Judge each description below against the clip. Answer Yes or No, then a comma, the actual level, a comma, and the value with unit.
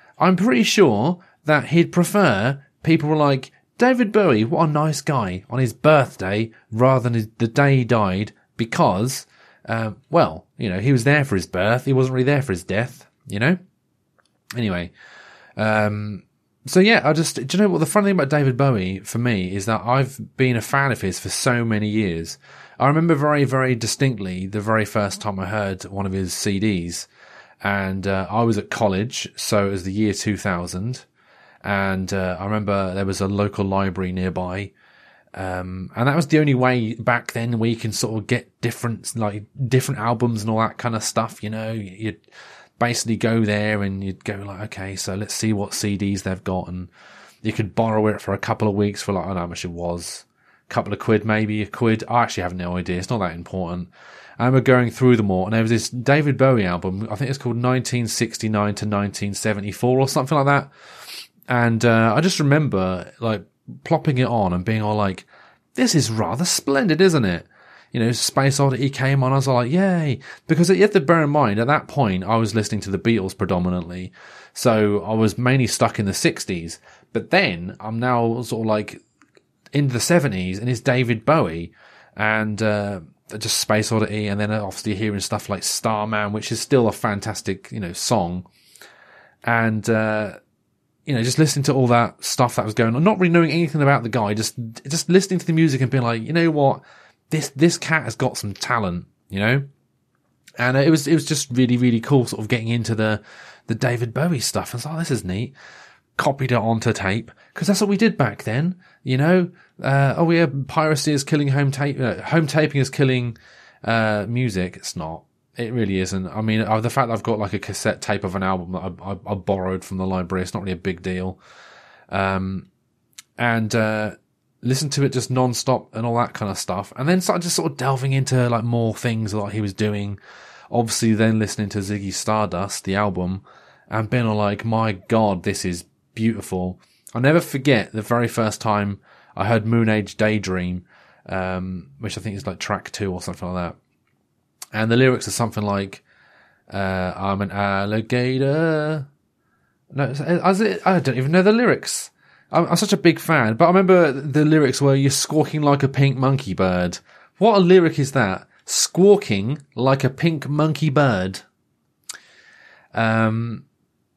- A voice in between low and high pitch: No, low, 115 Hz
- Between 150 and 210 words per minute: Yes, average, 200 wpm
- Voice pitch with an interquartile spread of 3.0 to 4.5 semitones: No, average, 5.2 semitones